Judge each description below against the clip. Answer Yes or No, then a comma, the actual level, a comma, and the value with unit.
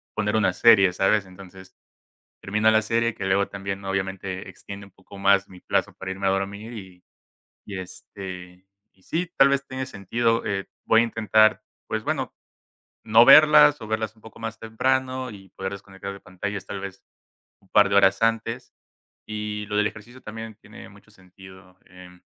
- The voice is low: Yes, low, 100 Hz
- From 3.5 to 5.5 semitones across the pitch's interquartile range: No, average, 2.7 semitones